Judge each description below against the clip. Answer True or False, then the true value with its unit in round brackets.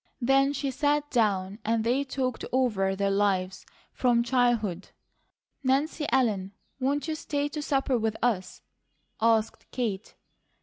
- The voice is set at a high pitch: True (240 Hz)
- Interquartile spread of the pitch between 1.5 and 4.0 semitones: False (4.9 semitones)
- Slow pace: True (130 wpm)